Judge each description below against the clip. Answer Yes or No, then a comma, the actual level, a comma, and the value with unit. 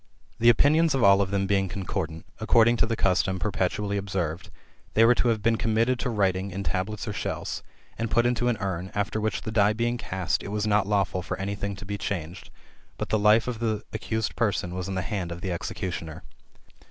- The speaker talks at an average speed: No, fast, 220 wpm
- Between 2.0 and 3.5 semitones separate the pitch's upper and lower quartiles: Yes, average, 3.0 semitones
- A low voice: Yes, low, 100 Hz